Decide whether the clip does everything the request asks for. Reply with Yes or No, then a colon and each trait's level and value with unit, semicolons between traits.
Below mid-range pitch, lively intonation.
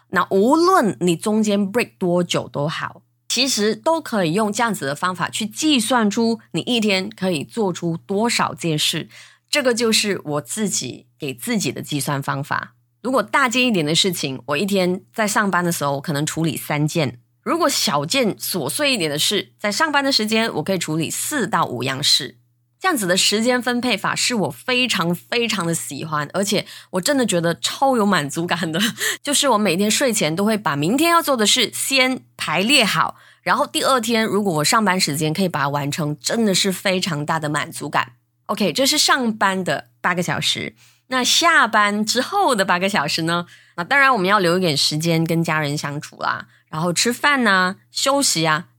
No: high, 190 Hz; wide, 6.8 semitones